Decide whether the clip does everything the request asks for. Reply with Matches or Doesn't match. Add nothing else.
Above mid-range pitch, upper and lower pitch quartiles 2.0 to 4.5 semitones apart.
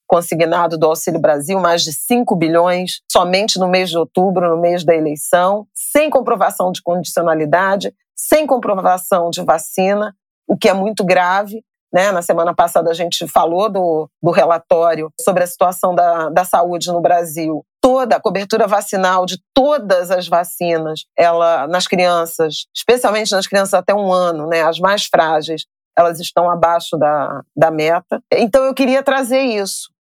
Doesn't match